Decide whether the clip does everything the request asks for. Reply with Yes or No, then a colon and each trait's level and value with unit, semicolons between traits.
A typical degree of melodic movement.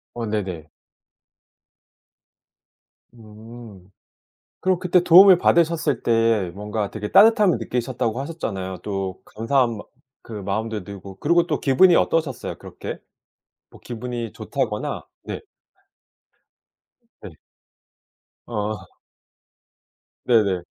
No: wide, 6.3 semitones